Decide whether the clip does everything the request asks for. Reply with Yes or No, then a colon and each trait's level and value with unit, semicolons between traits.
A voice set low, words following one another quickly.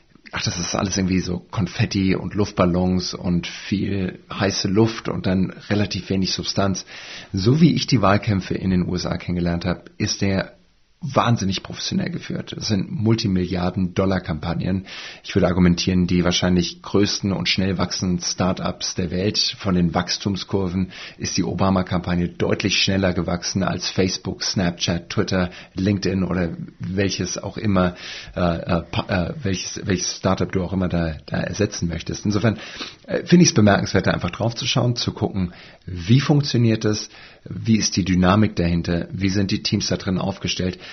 No: very low, 95 Hz; average, 160 wpm